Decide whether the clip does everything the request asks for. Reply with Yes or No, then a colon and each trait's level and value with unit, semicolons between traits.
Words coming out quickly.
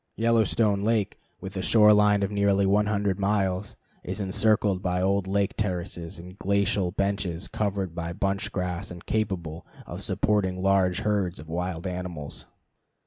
No: average, 145 wpm